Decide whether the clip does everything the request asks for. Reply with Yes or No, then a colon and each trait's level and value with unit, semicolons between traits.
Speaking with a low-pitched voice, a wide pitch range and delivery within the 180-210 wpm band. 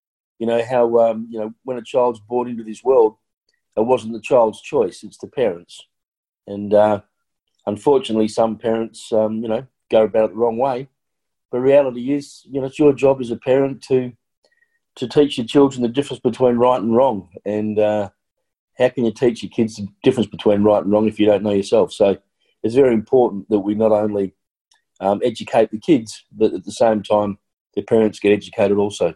No: low, 115 Hz; average, 3.2 semitones; average, 200 wpm